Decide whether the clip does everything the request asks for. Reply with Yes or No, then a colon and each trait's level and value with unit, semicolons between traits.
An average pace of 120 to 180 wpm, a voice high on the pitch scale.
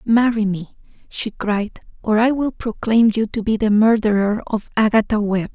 Yes: average, 175 wpm; high, 215 Hz